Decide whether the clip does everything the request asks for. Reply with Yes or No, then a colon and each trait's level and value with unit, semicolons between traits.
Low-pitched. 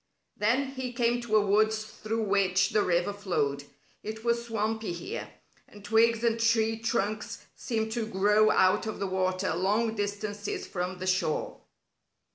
No: high, 215 Hz